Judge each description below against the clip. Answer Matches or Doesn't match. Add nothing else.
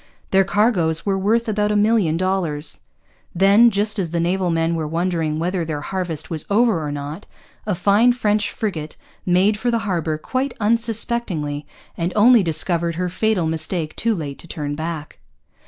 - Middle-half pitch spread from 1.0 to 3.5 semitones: Doesn't match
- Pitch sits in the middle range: Matches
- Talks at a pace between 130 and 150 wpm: Doesn't match